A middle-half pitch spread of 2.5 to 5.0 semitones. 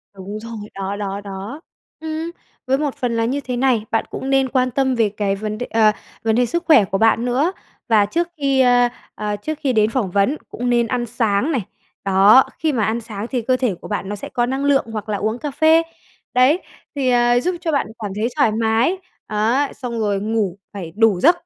Yes: average, 4.2 semitones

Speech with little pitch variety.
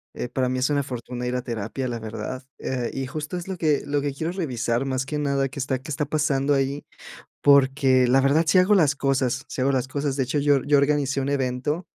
Yes: narrow, 2.2 semitones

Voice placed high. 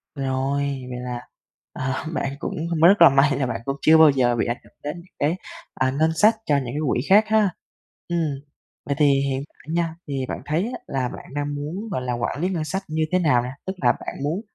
No: medium, 145 Hz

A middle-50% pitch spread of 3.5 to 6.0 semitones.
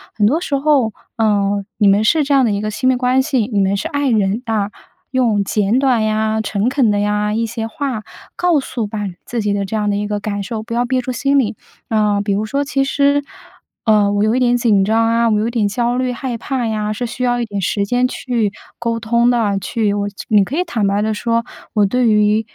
No: average, 3.1 semitones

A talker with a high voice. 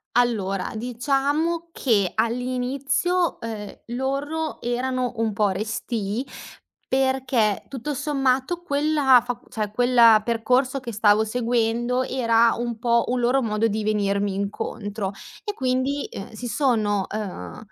Yes: high, 240 Hz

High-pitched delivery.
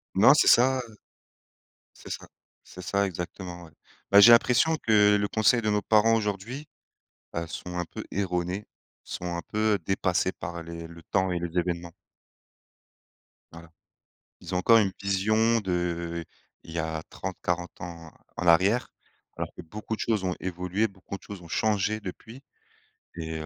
No: very low, 95 Hz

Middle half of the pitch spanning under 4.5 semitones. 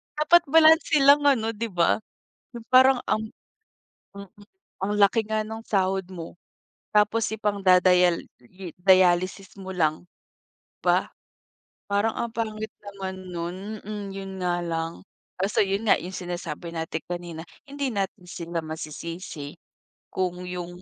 Yes: average, 3.7 semitones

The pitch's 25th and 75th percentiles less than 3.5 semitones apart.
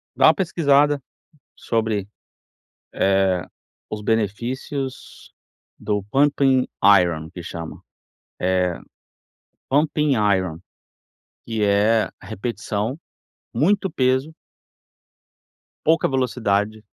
No: wide, 5.4 semitones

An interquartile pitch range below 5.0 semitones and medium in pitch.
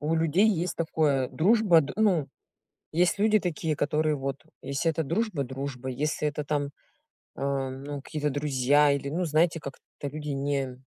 Yes: average, 2.9 semitones; medium, 150 Hz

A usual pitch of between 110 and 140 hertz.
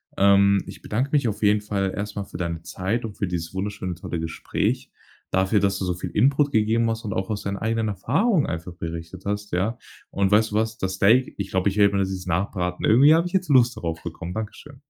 No: low, 100 Hz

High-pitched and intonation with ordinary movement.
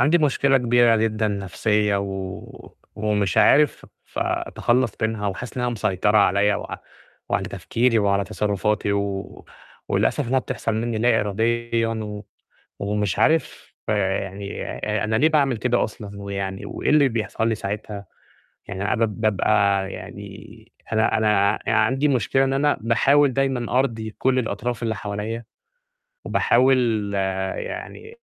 No: low, 110 Hz; average, 3.2 semitones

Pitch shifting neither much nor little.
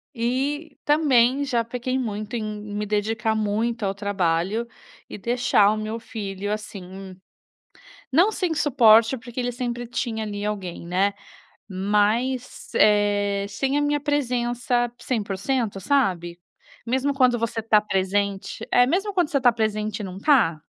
Yes: average, 3.7 semitones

